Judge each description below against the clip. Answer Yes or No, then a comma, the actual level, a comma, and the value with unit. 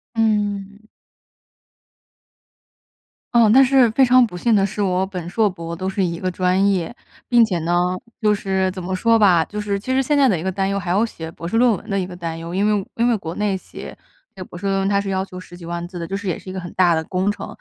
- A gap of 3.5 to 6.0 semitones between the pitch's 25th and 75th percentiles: No, average, 2.9 semitones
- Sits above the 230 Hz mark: No, high, 195 Hz